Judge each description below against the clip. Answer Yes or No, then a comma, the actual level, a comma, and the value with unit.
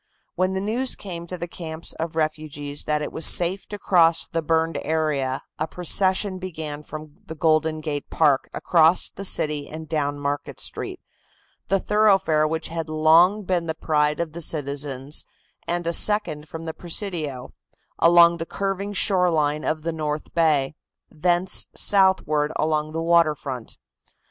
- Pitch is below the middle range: No, medium, 160 Hz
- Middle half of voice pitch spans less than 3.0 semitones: Yes, narrow, 2.6 semitones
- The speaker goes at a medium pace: Yes, average, 160 wpm